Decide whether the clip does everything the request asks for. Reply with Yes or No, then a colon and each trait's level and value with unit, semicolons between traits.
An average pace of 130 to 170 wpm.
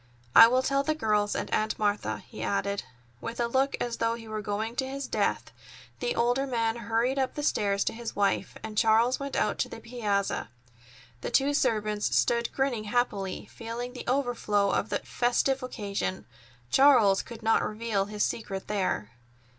No: average, 180 wpm